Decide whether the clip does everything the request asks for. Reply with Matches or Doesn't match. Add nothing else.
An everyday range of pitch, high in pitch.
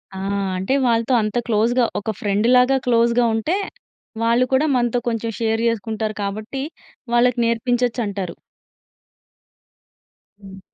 Doesn't match